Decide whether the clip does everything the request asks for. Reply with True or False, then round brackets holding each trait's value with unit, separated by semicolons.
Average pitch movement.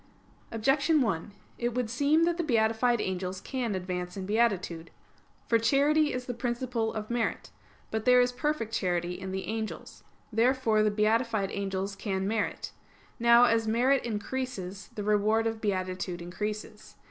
True (4.0 semitones)